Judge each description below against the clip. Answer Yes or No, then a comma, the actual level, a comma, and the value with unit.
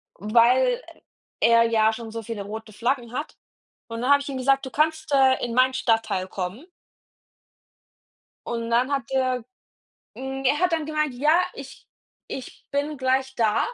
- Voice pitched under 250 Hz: No, very high, 255 Hz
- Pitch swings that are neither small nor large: Yes, average, 3.5 semitones